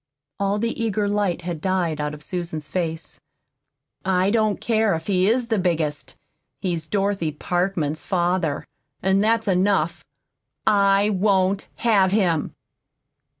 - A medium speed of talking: No, slow, 130 wpm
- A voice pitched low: No, high, 190 Hz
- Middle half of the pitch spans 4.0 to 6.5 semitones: No, average, 3.2 semitones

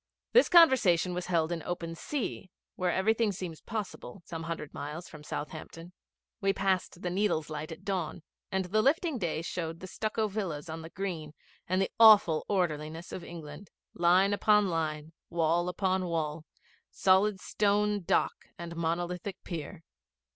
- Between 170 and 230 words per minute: No, average, 155 wpm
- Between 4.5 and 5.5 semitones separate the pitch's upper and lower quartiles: No, average, 3.3 semitones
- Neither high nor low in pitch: Yes, medium, 175 Hz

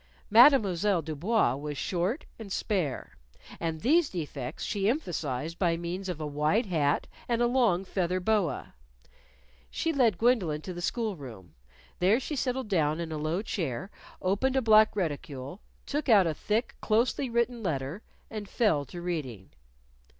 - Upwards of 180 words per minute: No, average, 155 wpm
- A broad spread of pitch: Yes, wide, 6.4 semitones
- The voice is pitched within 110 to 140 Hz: No, medium, 185 Hz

